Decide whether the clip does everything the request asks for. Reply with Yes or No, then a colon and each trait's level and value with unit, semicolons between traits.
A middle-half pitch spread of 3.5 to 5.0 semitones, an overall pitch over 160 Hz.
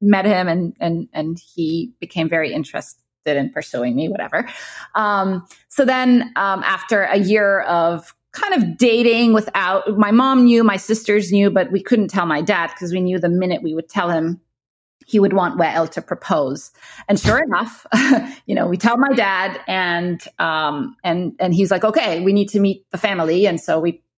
Yes: average, 4.1 semitones; high, 190 Hz